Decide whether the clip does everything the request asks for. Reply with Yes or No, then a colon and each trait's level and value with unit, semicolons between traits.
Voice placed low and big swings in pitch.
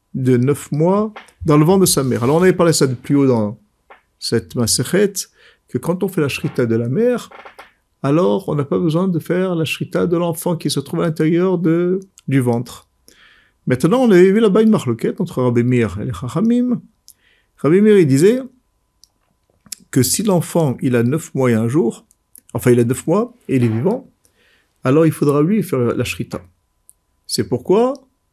No: medium, 160 Hz; wide, 7.0 semitones